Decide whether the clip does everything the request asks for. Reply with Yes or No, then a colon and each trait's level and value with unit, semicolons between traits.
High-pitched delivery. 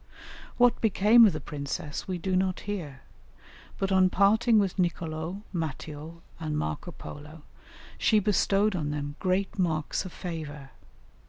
No: medium, 175 Hz